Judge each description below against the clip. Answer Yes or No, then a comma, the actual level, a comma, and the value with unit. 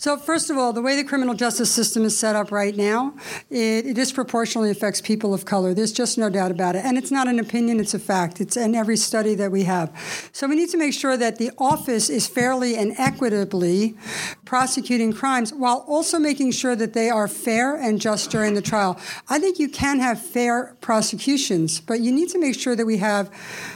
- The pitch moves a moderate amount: Yes, average, 3.6 semitones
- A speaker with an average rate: No, fast, 220 wpm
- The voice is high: Yes, high, 230 Hz